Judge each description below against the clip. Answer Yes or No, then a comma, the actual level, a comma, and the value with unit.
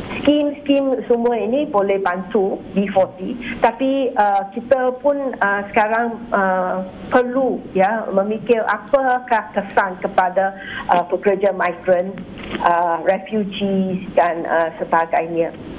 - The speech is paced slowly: No, average, 105 wpm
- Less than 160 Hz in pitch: No, high, 200 Hz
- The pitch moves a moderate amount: Yes, average, 4.5 semitones